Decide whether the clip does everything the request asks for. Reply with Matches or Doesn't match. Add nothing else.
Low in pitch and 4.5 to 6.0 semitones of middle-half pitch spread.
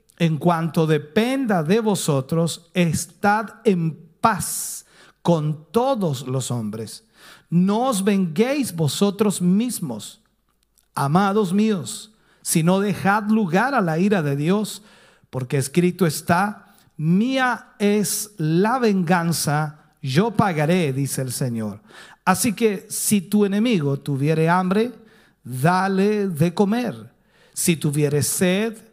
Doesn't match